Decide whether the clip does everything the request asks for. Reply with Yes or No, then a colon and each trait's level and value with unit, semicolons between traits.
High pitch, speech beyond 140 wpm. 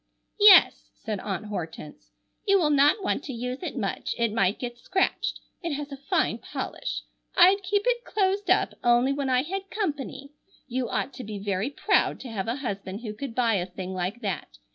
Yes: very high, 255 Hz; average, 195 wpm